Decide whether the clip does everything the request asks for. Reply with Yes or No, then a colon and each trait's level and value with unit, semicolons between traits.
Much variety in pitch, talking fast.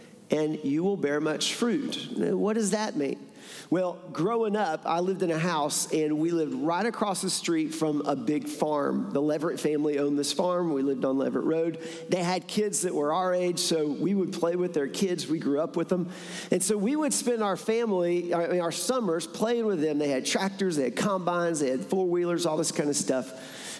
No: average, 4.0 semitones; fast, 215 wpm